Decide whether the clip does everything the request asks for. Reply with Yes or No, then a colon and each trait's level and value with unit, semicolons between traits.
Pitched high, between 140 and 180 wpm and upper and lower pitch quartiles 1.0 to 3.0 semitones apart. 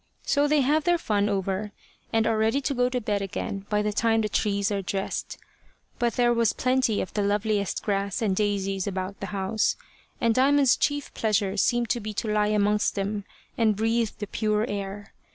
No: high, 210 Hz; average, 195 wpm; narrow, 2.6 semitones